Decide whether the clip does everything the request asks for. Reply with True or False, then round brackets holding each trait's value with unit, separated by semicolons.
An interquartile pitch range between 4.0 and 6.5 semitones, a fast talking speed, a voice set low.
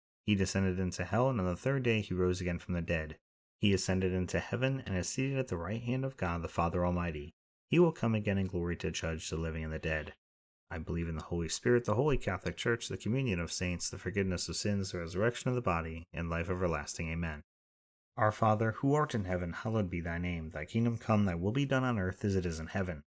True (4.6 semitones; 245 wpm; 90 Hz)